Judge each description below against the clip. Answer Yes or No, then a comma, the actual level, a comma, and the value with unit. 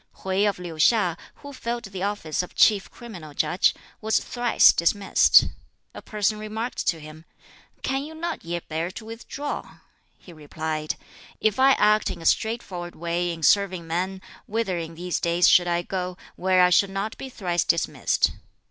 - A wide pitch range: No, average, 4.2 semitones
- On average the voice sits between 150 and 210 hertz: Yes, medium, 185 Hz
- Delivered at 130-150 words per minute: No, average, 170 wpm